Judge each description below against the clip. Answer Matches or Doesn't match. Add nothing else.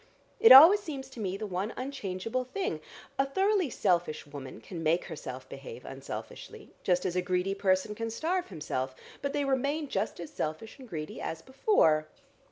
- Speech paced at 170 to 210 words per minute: Matches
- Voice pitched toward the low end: Doesn't match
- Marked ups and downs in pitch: Matches